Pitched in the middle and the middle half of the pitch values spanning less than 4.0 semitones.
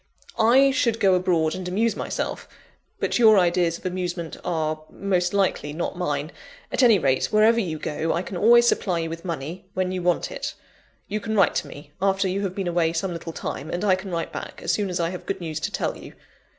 Yes: medium, 180 Hz; average, 3.1 semitones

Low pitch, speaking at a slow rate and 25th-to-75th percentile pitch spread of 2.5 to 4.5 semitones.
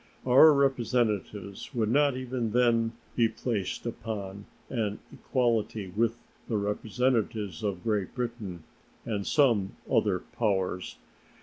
Yes: low, 110 Hz; slow, 115 wpm; average, 3.3 semitones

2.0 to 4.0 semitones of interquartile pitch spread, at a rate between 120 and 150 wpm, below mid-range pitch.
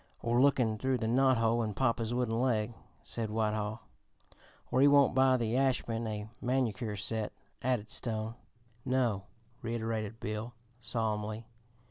Yes: narrow, 2.5 semitones; slow, 135 wpm; low, 115 Hz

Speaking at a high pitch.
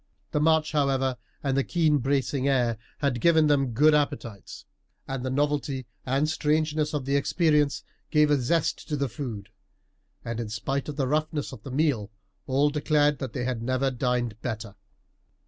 No: medium, 140 Hz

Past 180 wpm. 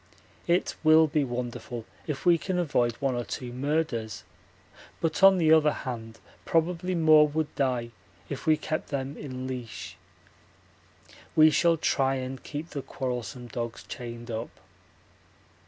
No: average, 140 wpm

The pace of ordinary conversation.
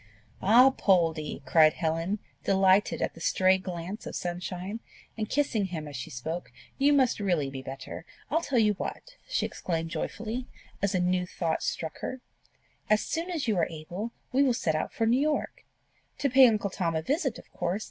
Yes: average, 190 wpm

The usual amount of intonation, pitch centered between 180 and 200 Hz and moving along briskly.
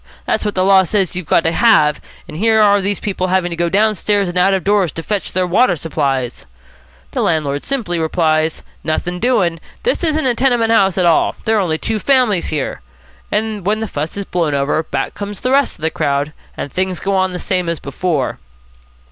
Yes: average, 4.4 semitones; medium, 185 Hz; fast, 215 wpm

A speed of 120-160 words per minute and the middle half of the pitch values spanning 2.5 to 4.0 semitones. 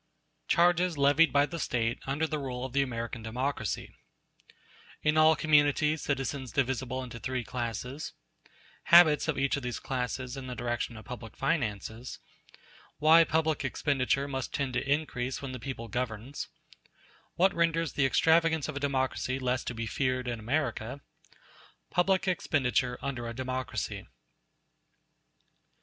Yes: slow, 135 wpm; average, 3.4 semitones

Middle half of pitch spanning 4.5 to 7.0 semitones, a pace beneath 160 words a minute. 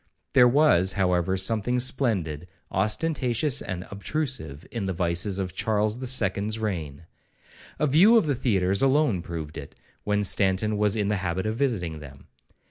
Yes: wide, 5.4 semitones; average, 150 wpm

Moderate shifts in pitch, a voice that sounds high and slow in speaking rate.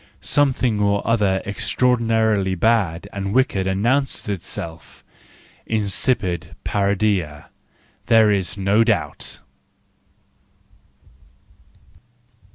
No: average, 3.1 semitones; low, 105 Hz; slow, 65 wpm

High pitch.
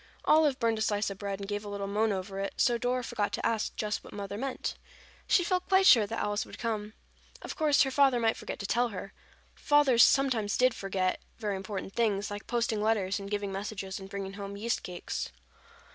Yes: high, 210 Hz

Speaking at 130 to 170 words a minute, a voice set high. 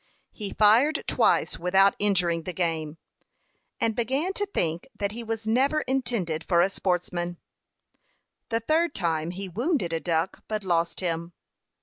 Yes: average, 145 wpm; high, 195 Hz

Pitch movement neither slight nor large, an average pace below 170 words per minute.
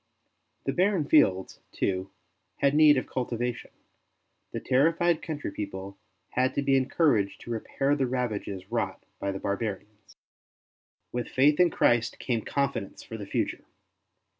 No: wide, 5.8 semitones; average, 140 wpm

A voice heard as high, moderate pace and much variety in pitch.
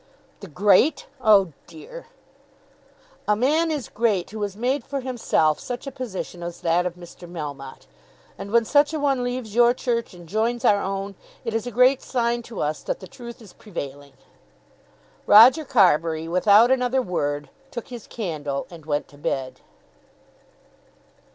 Yes: high, 215 Hz; average, 160 wpm; wide, 6.2 semitones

